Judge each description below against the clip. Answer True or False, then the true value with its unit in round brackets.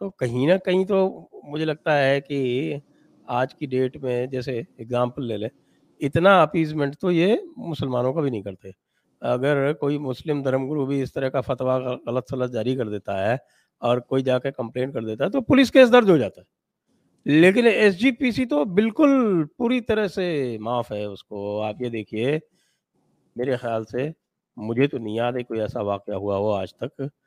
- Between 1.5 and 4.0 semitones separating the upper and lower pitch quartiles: False (4.8 semitones)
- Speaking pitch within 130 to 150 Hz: True (135 Hz)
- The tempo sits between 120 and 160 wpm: False (185 wpm)